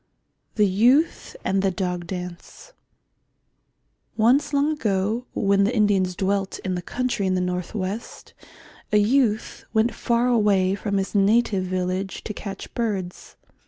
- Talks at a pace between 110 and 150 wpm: Yes, average, 140 wpm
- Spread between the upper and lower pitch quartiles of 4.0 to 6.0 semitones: No, average, 3.6 semitones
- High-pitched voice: Yes, high, 200 Hz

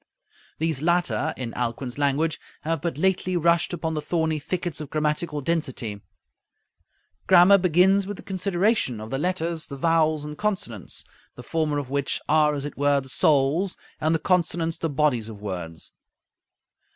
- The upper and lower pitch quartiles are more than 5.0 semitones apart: No, average, 3.8 semitones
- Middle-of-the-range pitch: Yes, medium, 155 Hz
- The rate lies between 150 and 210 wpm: Yes, average, 160 wpm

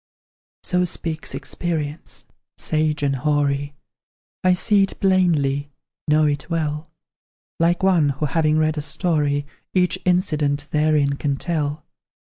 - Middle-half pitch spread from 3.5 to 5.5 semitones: No, average, 2.9 semitones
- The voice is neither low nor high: Yes, medium, 155 Hz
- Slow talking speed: Yes, slow, 120 wpm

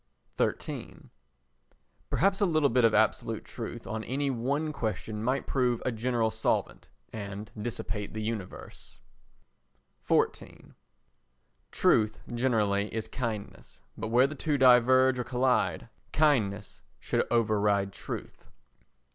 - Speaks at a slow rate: Yes, slow, 115 wpm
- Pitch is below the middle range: Yes, low, 115 Hz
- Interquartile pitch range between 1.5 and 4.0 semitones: Yes, average, 3.6 semitones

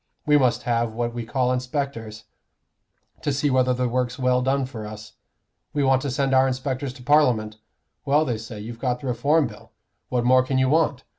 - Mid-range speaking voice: No, low, 125 Hz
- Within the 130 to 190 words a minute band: No, average, 200 wpm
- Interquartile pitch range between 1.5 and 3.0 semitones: Yes, narrow, 2.5 semitones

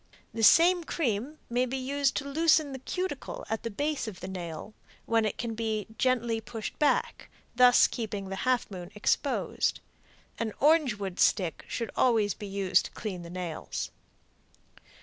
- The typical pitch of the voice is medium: No, high, 230 Hz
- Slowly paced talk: No, average, 165 wpm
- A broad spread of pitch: No, average, 5.0 semitones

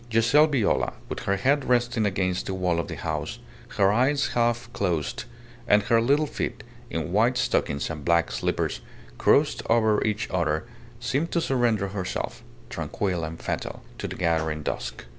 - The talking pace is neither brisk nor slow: Yes, average, 160 wpm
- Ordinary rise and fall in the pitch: No, wide, 6.0 semitones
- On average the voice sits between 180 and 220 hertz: No, low, 105 Hz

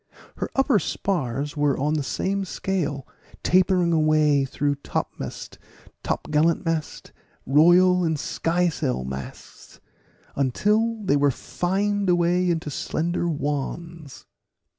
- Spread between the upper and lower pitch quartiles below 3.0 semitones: No, average, 3.8 semitones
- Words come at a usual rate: No, slow, 100 wpm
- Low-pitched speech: No, medium, 165 Hz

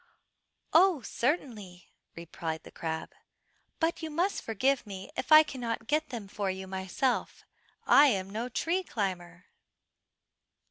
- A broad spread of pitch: Yes, wide, 7.9 semitones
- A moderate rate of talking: No, slow, 130 wpm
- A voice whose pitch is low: No, high, 225 Hz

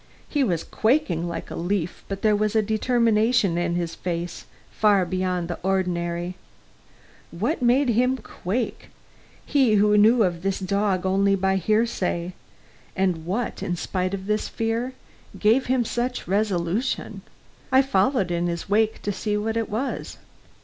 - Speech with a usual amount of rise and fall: Yes, average, 4.1 semitones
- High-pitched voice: Yes, high, 200 Hz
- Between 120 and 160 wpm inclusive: Yes, average, 150 wpm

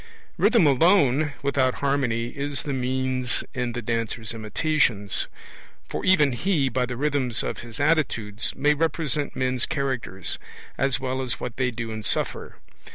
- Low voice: Yes, low, 130 Hz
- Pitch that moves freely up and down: No, average, 3.4 semitones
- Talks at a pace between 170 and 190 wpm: No, average, 150 wpm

